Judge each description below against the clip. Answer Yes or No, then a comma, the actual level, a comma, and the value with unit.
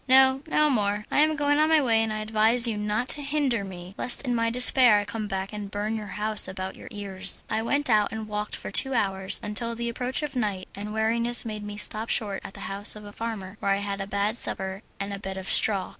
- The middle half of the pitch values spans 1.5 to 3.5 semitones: Yes, average, 3.0 semitones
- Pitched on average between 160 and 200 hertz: No, high, 215 Hz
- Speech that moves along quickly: Yes, fast, 250 wpm